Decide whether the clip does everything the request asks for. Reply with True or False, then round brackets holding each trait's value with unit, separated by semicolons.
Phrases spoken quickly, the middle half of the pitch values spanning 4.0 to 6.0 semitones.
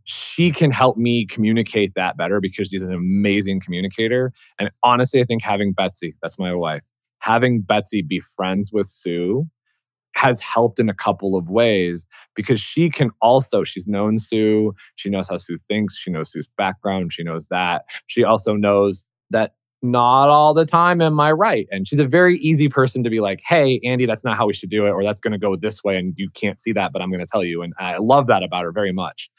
True (220 wpm; 4.4 semitones)